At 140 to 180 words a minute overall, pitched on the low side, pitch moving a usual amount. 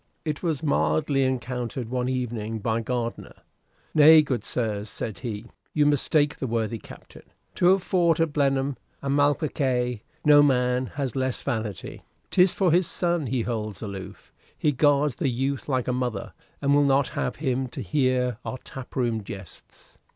Yes: average, 165 wpm; low, 130 Hz; average, 3.8 semitones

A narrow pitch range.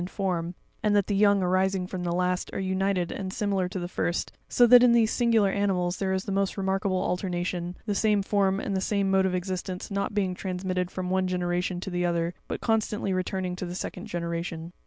Yes: narrow, 1.7 semitones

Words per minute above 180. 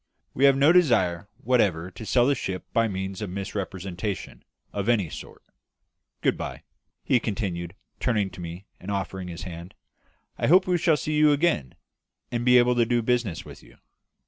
No: average, 175 wpm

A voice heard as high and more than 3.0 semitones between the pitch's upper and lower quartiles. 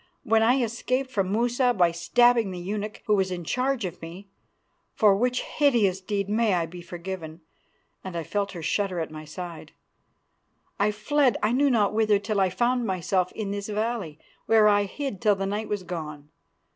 Yes: high, 205 Hz; average, 4.2 semitones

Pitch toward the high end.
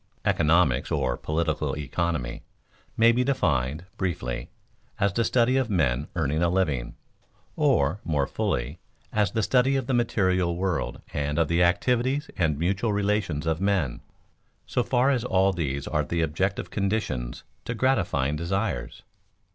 No: very low, 90 Hz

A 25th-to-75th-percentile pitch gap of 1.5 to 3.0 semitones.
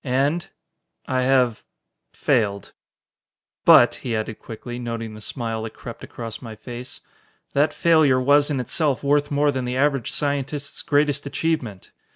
No: average, 3.7 semitones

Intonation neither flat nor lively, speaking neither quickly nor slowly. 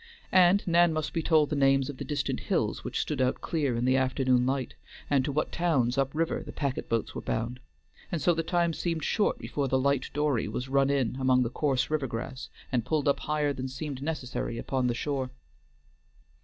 No: average, 3.0 semitones; fast, 210 wpm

